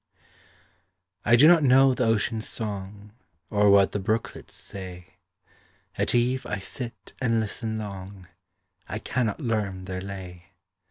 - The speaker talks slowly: Yes, slow, 130 wpm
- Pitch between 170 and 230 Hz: No, low, 105 Hz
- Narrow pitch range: No, average, 3.7 semitones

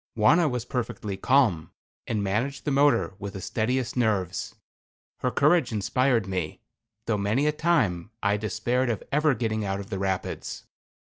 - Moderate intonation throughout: Yes, average, 4.9 semitones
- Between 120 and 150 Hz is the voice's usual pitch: No, low, 110 Hz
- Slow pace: No, average, 160 wpm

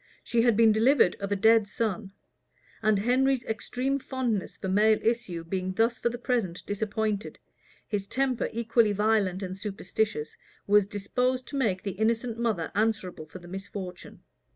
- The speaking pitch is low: No, high, 215 Hz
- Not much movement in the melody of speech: No, average, 3.3 semitones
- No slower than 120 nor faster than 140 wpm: No, average, 155 wpm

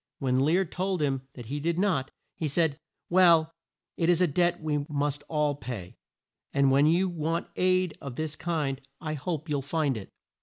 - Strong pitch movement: No, average, 3.6 semitones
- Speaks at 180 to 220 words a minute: Yes, average, 185 wpm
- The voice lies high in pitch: No, medium, 155 Hz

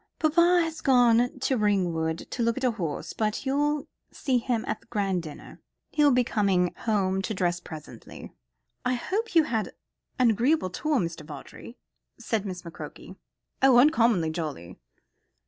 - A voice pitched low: No, high, 225 Hz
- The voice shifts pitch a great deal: Yes, wide, 6.8 semitones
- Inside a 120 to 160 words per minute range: Yes, average, 155 wpm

